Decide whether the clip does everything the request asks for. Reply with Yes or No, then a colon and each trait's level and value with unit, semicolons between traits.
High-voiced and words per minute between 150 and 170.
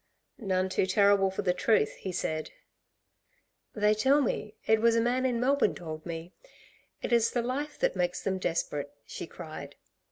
Yes: high, 205 Hz; average, 165 wpm